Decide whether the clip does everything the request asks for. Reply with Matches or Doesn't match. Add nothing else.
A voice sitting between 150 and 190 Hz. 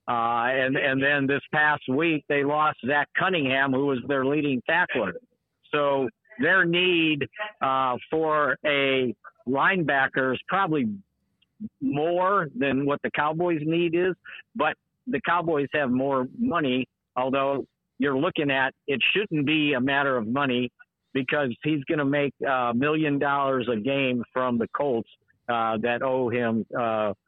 Doesn't match